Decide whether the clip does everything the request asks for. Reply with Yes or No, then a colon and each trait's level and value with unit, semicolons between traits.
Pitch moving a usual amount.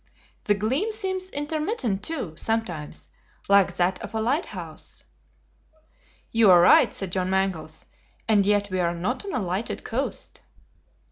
No: wide, 6.6 semitones